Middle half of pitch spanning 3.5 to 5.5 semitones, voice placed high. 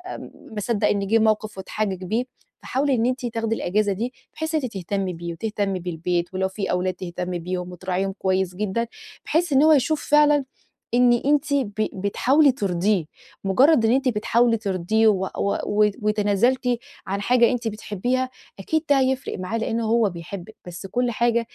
Yes: average, 4.6 semitones; high, 215 Hz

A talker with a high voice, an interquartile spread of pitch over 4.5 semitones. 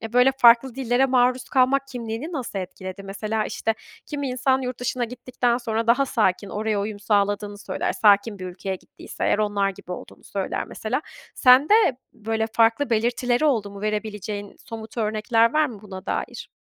No: high, 225 Hz; average, 3.5 semitones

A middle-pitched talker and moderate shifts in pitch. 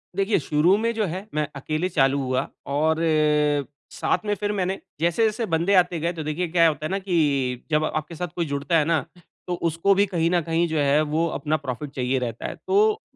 Yes: medium, 160 Hz; average, 3.5 semitones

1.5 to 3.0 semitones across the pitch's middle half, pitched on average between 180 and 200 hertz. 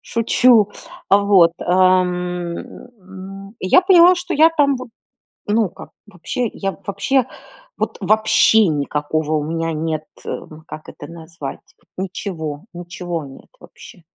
No: average, 4.7 semitones; medium, 185 Hz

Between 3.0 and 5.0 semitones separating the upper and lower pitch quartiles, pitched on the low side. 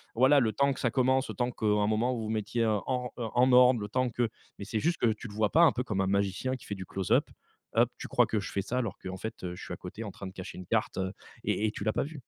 Yes: average, 3.7 semitones; low, 110 Hz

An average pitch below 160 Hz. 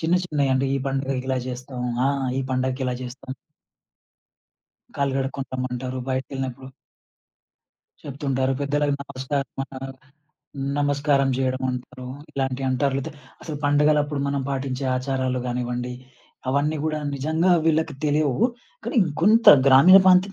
Yes: low, 135 Hz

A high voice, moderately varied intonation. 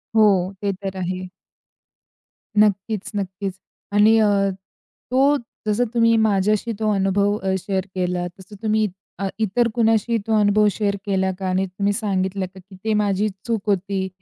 No: high, 205 Hz; narrow, 2.2 semitones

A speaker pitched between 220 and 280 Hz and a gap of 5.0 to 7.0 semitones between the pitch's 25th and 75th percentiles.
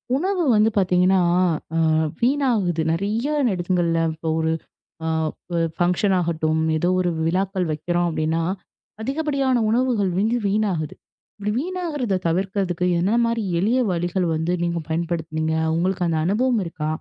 No: medium, 185 Hz; wide, 5.4 semitones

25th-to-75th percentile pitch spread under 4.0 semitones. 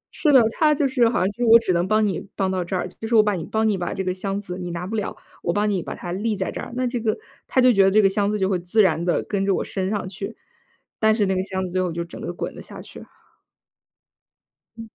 Yes: average, 3.0 semitones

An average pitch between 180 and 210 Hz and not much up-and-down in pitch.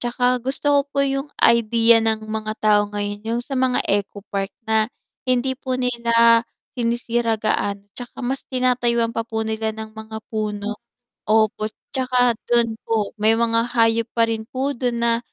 No: high, 230 Hz; narrow, 2.0 semitones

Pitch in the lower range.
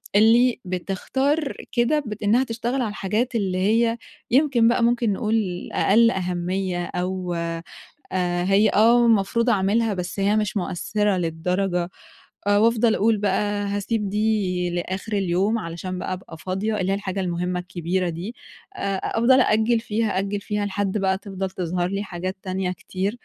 No: high, 200 Hz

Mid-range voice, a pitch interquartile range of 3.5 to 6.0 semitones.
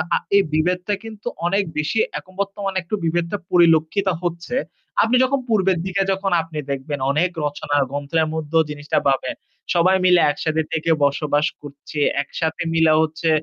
Yes: medium, 165 Hz; average, 3.8 semitones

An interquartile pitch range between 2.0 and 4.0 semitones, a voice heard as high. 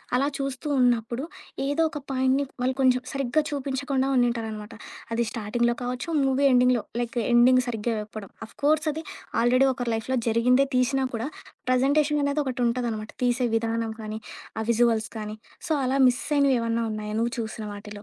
Yes: average, 2.8 semitones; high, 245 Hz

